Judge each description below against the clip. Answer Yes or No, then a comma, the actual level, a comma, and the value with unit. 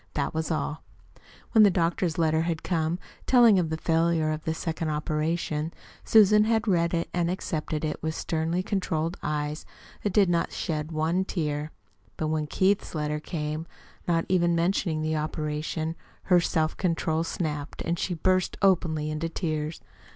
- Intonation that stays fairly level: Yes, narrow, 2.2 semitones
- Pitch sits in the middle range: Yes, medium, 165 Hz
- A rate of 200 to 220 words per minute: No, average, 160 wpm